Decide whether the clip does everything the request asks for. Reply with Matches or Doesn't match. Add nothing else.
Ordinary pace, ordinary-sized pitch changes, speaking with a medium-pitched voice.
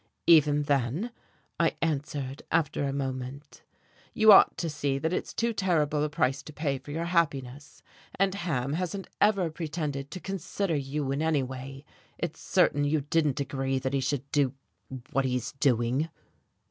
Matches